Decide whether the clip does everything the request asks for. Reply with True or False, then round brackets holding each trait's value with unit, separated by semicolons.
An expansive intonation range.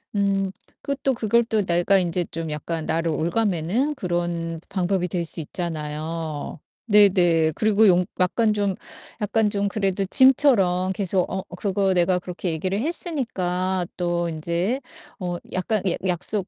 False (3.1 semitones)